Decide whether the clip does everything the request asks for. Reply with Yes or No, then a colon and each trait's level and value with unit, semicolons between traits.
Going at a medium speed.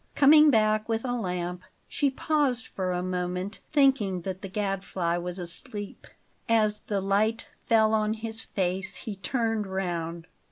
Yes: average, 150 wpm